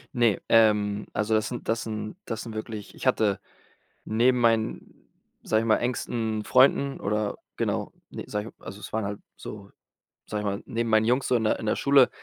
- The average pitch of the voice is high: No, low, 110 Hz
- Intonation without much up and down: Yes, narrow, 1.8 semitones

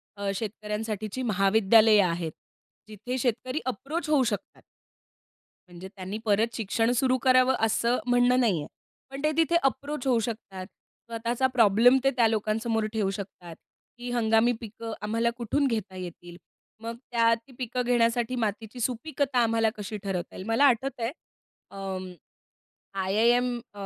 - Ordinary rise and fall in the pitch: Yes, average, 3.1 semitones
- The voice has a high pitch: Yes, high, 230 Hz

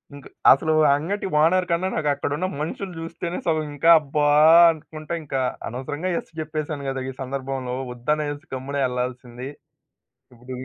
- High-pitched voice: No, medium, 145 Hz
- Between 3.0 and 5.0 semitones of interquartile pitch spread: Yes, average, 3.4 semitones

